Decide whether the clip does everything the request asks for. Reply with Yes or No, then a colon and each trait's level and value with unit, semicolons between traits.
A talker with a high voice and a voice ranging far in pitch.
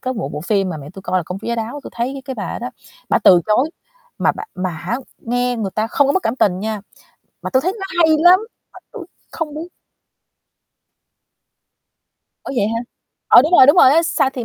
Yes: high, 240 Hz; wide, 6.4 semitones